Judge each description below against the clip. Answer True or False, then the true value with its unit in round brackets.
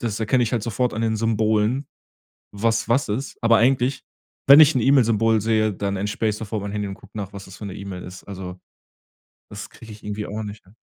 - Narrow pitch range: True (2.2 semitones)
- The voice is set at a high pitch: False (110 Hz)